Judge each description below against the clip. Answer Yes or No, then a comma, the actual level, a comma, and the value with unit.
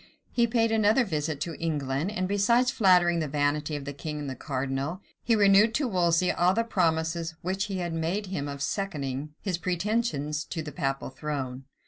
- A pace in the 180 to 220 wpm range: Yes, average, 185 wpm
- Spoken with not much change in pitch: No, average, 5.2 semitones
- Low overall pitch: No, medium, 165 Hz